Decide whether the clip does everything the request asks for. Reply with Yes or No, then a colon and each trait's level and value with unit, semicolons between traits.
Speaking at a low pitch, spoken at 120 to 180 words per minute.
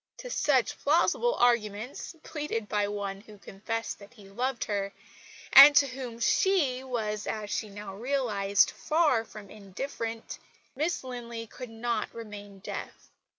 No: high, 230 Hz; average, 140 wpm